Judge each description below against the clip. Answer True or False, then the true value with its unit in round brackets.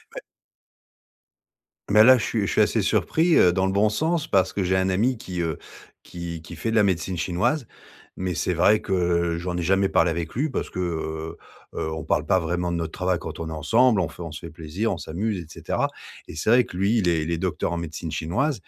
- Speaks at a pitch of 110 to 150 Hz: False (90 Hz)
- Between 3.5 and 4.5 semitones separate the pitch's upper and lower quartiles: True (4.2 semitones)